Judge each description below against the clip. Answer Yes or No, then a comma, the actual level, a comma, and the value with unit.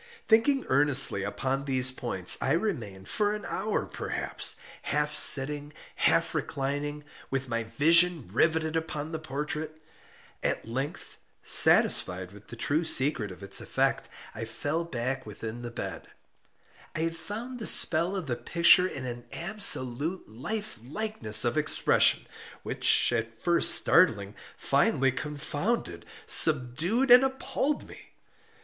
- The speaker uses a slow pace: Yes, slow, 130 wpm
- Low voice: No, medium, 145 Hz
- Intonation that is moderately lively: No, wide, 6.0 semitones